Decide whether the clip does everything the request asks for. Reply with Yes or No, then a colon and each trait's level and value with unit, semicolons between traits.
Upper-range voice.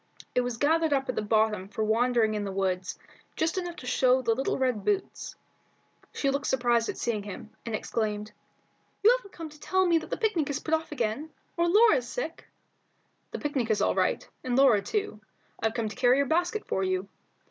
Yes: very high, 250 Hz